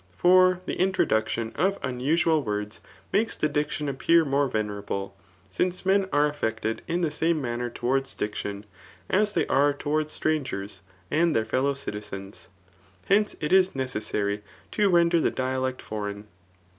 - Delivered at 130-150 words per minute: Yes, average, 145 wpm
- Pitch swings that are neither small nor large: No, wide, 7.5 semitones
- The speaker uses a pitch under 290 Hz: Yes, medium, 140 Hz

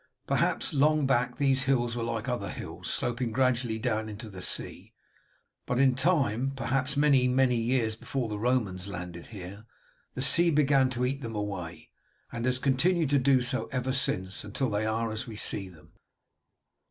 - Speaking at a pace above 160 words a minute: Yes, average, 175 wpm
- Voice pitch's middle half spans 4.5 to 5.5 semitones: No, average, 3.6 semitones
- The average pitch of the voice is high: No, low, 125 Hz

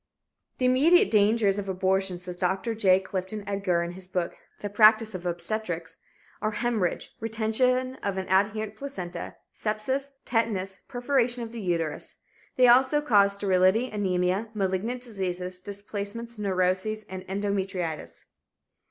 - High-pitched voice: Yes, high, 200 Hz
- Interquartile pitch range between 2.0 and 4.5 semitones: Yes, average, 3.4 semitones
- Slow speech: Yes, slow, 130 wpm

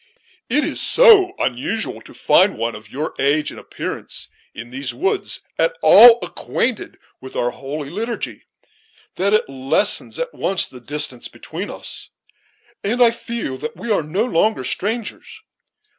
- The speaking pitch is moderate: Yes, medium, 175 Hz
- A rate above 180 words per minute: No, average, 150 wpm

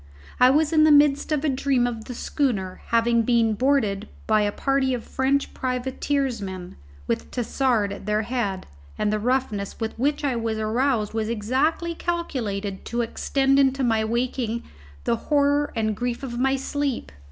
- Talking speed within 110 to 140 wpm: No, average, 165 wpm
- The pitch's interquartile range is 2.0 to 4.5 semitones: Yes, average, 4.0 semitones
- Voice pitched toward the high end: Yes, high, 245 Hz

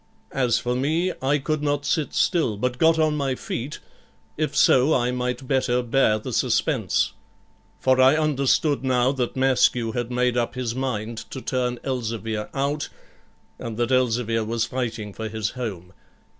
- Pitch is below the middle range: Yes, low, 125 Hz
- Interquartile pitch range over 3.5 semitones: No, average, 2.7 semitones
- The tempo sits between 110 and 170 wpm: Yes, average, 160 wpm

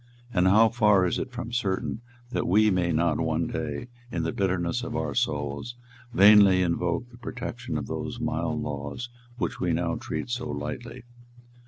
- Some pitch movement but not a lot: No, wide, 6.1 semitones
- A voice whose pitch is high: No, very low, 95 Hz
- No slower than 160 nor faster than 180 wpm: Yes, average, 170 wpm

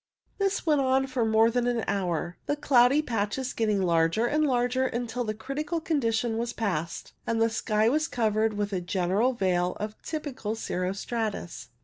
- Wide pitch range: No, average, 4.1 semitones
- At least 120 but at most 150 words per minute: No, average, 170 wpm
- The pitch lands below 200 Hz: No, high, 225 Hz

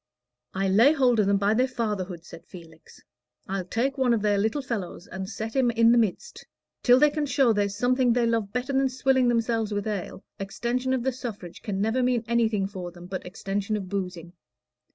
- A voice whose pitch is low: No, high, 220 Hz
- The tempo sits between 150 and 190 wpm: No, fast, 205 wpm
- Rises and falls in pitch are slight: No, average, 4.2 semitones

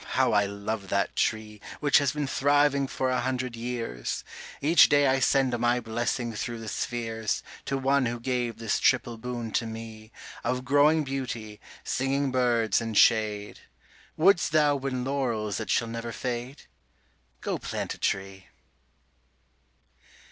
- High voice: No, low, 120 Hz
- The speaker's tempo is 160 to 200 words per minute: No, average, 150 wpm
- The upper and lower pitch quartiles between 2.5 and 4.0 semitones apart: Yes, average, 3.2 semitones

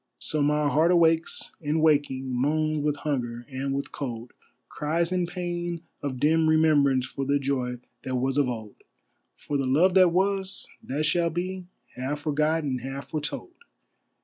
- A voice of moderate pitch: Yes, medium, 150 Hz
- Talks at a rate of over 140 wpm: Yes, average, 160 wpm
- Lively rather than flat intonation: No, average, 3.5 semitones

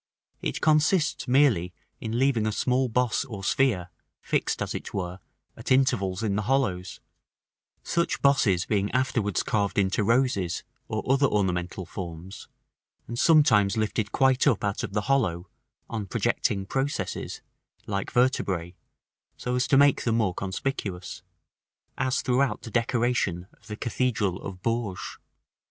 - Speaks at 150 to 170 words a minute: No, average, 140 wpm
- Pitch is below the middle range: Yes, low, 110 Hz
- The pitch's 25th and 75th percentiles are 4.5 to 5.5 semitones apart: Yes, average, 5.1 semitones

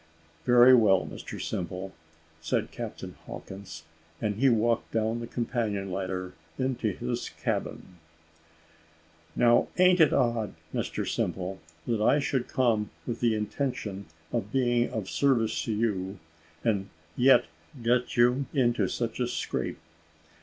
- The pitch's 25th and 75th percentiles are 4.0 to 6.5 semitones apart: No, average, 3.4 semitones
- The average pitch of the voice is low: Yes, low, 115 Hz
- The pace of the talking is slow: Yes, slow, 130 wpm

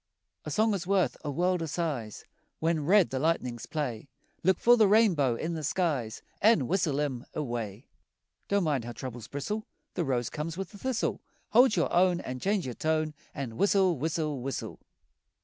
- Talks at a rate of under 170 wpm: No, average, 180 wpm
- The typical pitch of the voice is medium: Yes, medium, 160 Hz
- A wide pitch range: Yes, wide, 6.2 semitones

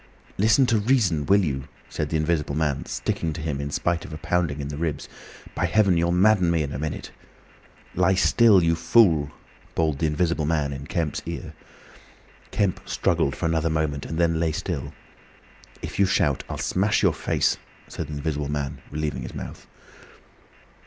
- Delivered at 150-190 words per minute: Yes, average, 180 wpm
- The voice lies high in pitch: No, very low, 80 Hz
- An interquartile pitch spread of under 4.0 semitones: Yes, average, 3.3 semitones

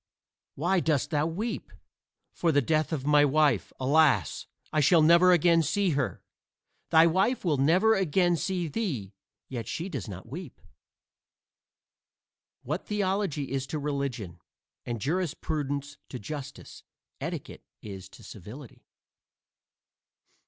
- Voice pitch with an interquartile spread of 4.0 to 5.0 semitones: Yes, average, 4.4 semitones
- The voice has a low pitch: No, medium, 150 Hz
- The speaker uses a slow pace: Yes, slow, 125 wpm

